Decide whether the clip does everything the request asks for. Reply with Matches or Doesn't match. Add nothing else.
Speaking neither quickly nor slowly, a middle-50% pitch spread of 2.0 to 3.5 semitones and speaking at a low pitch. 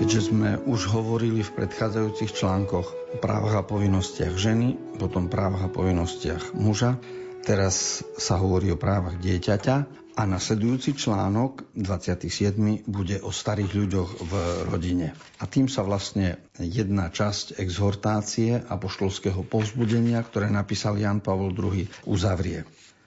Matches